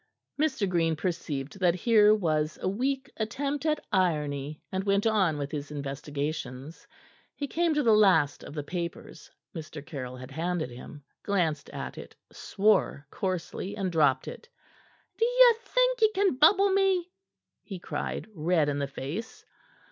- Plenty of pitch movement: Yes, wide, 7.9 semitones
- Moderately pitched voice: Yes, medium, 180 Hz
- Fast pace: No, average, 150 wpm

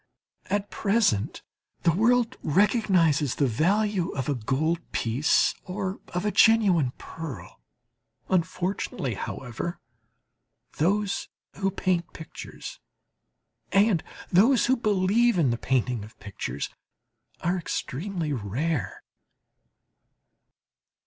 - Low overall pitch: No, medium, 175 Hz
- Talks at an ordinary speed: No, slow, 95 wpm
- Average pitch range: No, wide, 7.0 semitones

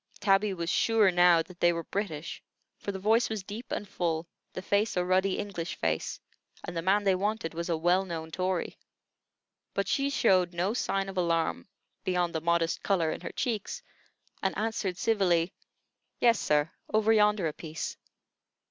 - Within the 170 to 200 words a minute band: Yes, average, 175 wpm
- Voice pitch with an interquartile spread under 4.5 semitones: Yes, average, 3.3 semitones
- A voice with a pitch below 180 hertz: No, medium, 185 Hz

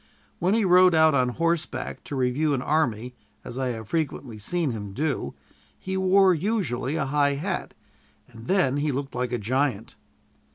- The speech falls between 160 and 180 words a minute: Yes, average, 170 wpm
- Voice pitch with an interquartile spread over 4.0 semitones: Yes, average, 5.2 semitones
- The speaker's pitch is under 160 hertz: Yes, medium, 140 Hz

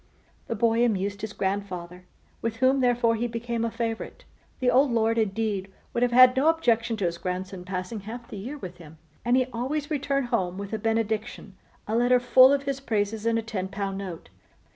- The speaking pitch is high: Yes, high, 225 Hz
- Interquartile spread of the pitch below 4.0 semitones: Yes, average, 3.6 semitones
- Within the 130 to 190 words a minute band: No, average, 200 wpm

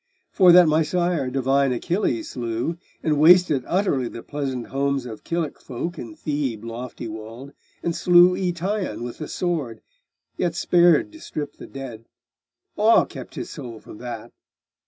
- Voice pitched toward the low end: No, medium, 145 Hz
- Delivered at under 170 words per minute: Yes, average, 155 wpm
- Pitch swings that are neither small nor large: No, wide, 6.1 semitones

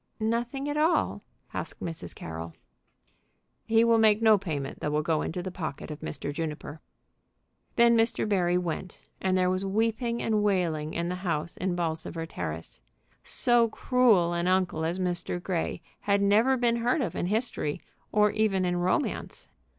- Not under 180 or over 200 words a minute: No, average, 165 wpm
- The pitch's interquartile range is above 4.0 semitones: Yes, average, 5.3 semitones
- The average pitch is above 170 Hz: Yes, medium, 185 Hz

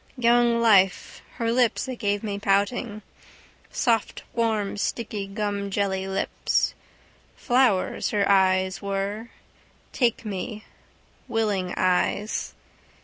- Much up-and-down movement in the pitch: No, average, 2.9 semitones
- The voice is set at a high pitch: Yes, high, 205 Hz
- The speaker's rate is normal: No, slow, 95 wpm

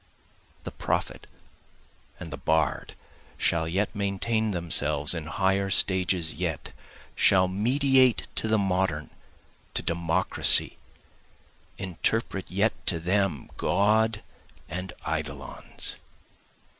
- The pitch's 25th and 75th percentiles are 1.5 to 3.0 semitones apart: No, average, 3.8 semitones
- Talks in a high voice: No, very low, 95 Hz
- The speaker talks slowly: Yes, slow, 95 wpm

